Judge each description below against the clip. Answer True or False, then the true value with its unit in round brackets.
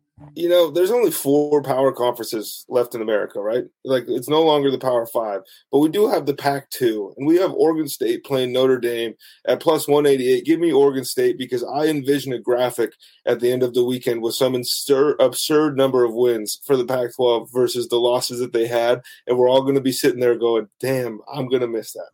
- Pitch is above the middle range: False (135 Hz)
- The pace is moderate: False (225 wpm)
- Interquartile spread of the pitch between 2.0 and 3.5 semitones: False (4.8 semitones)